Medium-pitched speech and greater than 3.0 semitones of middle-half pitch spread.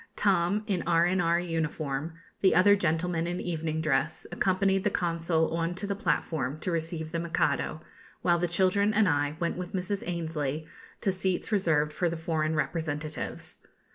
No: medium, 170 Hz; narrow, 2.5 semitones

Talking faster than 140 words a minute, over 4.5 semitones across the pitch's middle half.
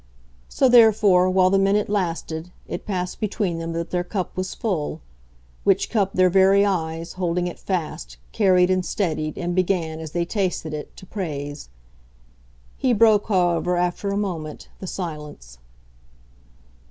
No: average, 150 wpm; average, 2.9 semitones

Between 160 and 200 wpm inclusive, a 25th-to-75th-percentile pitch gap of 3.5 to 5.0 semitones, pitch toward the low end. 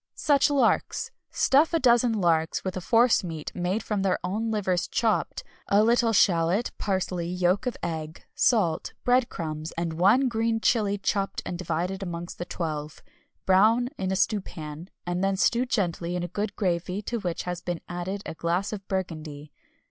No: average, 170 wpm; average, 4.2 semitones; high, 190 Hz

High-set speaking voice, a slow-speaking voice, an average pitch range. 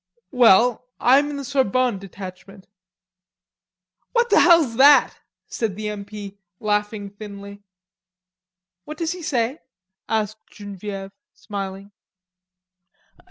Yes: high, 215 Hz; slow, 105 wpm; average, 4.2 semitones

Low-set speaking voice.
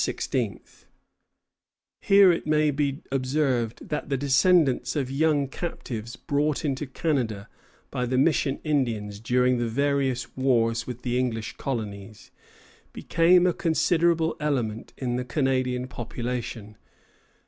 Yes: low, 130 Hz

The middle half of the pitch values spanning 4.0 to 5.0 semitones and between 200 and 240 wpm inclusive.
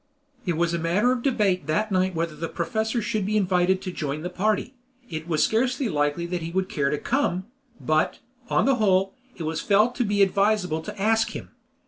Yes: average, 4.4 semitones; fast, 205 wpm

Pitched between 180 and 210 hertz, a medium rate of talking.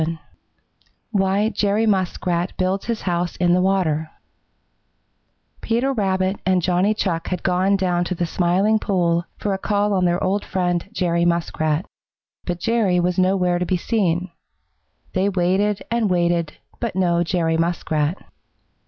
Yes: medium, 185 Hz; average, 145 wpm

